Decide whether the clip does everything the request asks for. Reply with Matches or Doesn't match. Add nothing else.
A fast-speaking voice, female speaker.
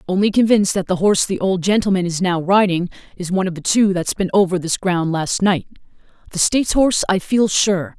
Matches